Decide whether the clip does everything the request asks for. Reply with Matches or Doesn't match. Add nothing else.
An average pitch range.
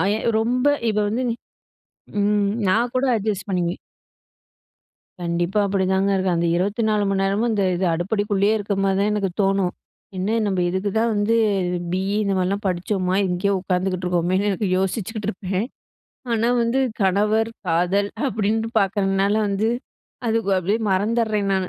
Doesn't match